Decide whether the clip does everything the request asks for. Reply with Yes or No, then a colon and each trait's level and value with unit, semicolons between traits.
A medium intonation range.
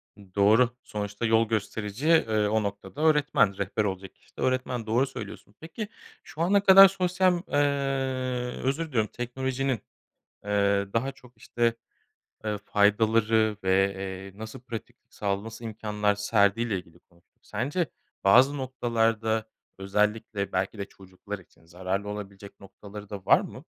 Yes: average, 4.2 semitones